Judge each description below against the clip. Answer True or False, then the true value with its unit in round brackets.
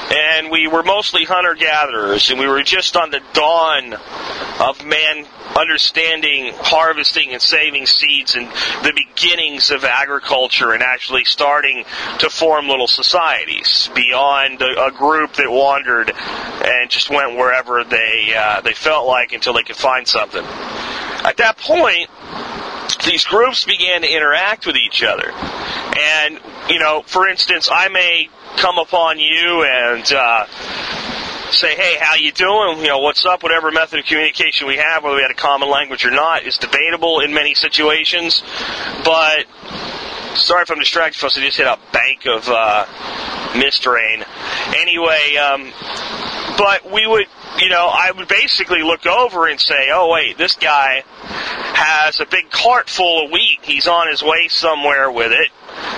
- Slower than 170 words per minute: True (160 wpm)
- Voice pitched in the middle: True (155 Hz)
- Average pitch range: True (3.2 semitones)